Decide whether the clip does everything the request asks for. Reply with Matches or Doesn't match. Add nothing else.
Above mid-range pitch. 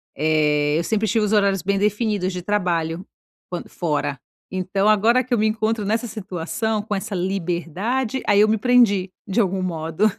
Matches